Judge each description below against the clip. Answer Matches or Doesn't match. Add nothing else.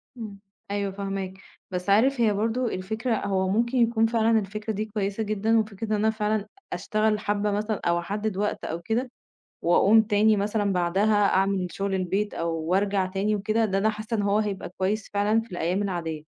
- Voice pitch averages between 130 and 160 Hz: Doesn't match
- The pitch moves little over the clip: Matches